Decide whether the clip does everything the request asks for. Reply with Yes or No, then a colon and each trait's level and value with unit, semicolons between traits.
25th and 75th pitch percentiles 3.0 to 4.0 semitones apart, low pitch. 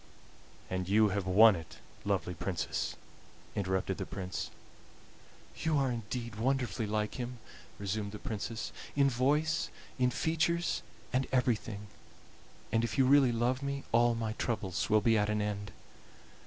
Yes: average, 3.7 semitones; low, 115 Hz